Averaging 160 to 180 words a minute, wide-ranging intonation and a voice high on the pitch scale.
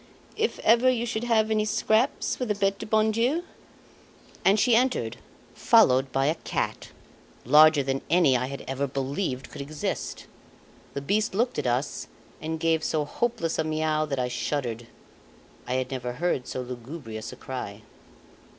No: average, 170 wpm; wide, 8.6 semitones; medium, 155 Hz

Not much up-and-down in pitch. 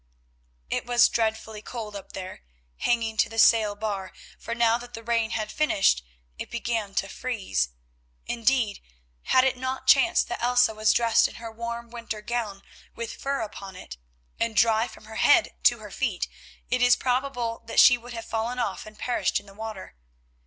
Yes: narrow, 2.0 semitones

